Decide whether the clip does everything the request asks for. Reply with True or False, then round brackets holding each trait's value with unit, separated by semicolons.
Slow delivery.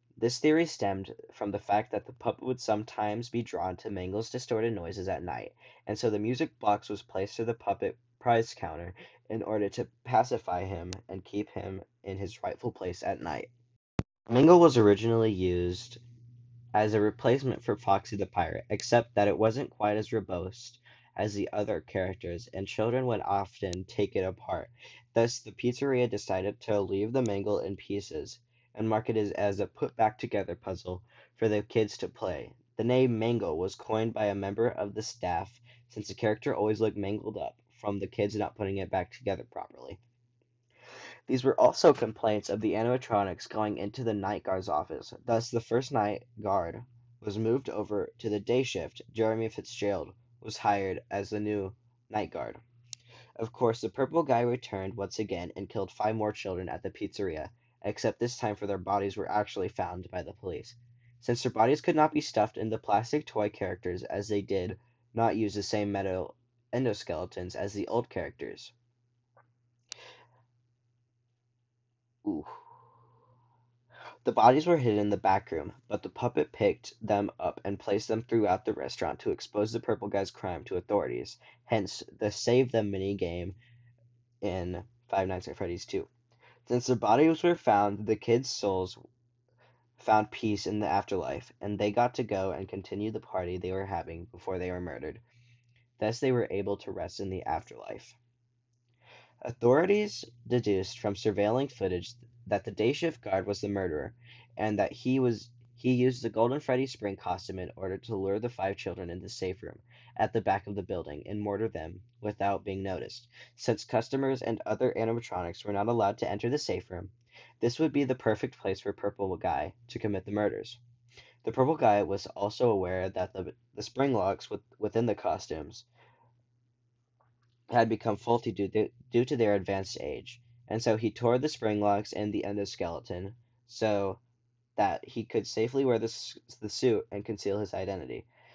False (180 wpm)